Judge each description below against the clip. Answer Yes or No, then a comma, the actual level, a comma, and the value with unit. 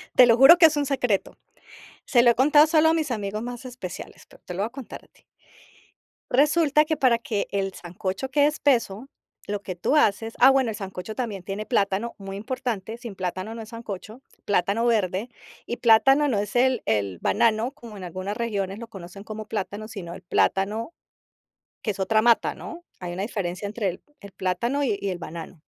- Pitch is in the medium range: No, high, 220 Hz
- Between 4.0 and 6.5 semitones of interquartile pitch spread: Yes, average, 4.5 semitones